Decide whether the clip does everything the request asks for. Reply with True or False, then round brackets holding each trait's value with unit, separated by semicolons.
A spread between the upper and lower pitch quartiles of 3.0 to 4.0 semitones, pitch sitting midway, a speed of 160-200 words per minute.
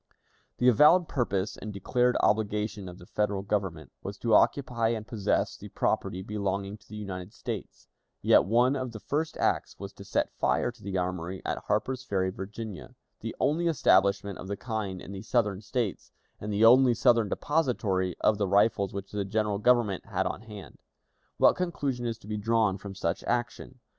False (3.5 semitones; 105 Hz; 185 wpm)